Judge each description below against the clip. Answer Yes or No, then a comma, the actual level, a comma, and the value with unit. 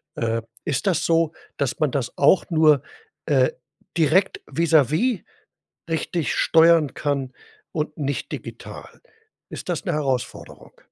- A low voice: No, medium, 155 Hz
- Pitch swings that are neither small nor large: Yes, average, 3.0 semitones